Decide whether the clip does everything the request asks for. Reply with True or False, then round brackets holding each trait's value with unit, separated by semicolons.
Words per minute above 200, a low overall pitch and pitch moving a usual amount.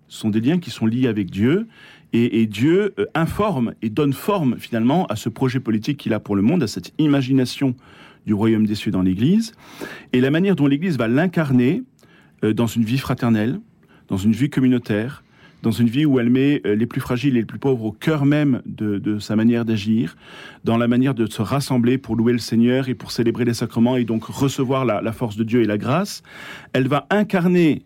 True (220 wpm; 125 Hz; 3.7 semitones)